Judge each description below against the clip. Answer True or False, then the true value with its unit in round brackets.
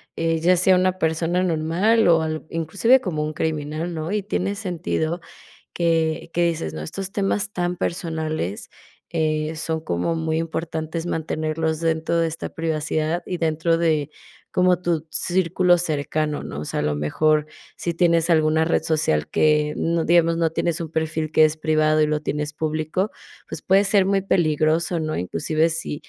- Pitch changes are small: True (1.8 semitones)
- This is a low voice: False (160 Hz)